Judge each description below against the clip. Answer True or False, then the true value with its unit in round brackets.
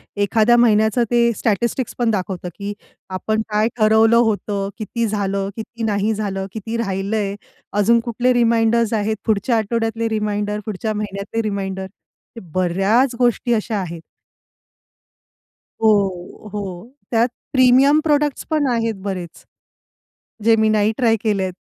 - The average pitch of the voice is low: False (220 Hz)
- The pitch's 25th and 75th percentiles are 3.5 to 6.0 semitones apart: False (2.5 semitones)